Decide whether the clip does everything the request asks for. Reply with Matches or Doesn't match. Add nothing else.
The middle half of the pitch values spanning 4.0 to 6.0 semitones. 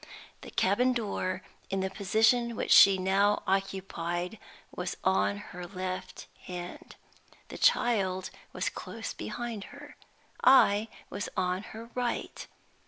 Doesn't match